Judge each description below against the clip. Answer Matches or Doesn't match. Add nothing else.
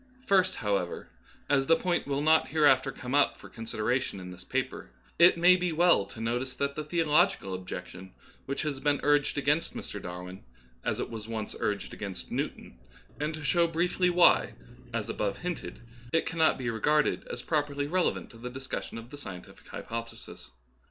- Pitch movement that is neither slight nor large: Doesn't match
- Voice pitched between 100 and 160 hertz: Matches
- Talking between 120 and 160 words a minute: Doesn't match